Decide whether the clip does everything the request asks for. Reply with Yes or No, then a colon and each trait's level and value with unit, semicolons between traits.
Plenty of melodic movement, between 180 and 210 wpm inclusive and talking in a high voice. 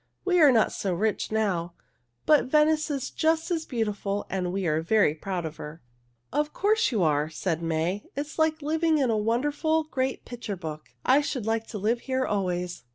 Yes: wide, 8.6 semitones; average, 195 wpm; high, 225 Hz